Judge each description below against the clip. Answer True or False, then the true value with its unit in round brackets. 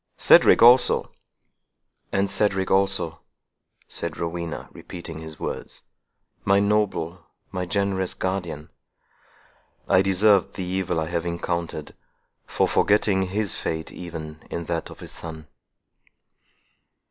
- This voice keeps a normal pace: False (110 wpm)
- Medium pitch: False (90 Hz)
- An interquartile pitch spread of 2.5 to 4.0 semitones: True (2.9 semitones)